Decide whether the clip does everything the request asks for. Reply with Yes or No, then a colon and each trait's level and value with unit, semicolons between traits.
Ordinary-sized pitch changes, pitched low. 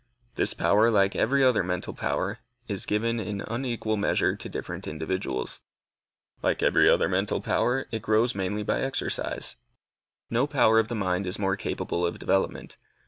Yes: average, 3.4 semitones; low, 105 Hz